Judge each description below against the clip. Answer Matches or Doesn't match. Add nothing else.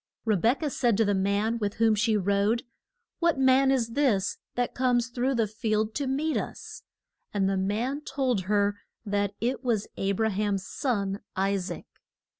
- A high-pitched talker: Matches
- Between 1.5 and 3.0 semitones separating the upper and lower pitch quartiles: Doesn't match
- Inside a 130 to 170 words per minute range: Doesn't match